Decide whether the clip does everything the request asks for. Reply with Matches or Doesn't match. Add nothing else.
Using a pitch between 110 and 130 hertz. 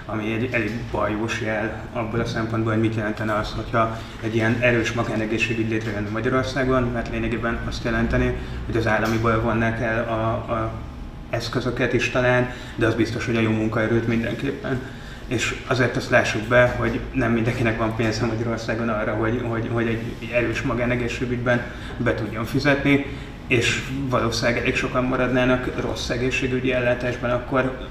Matches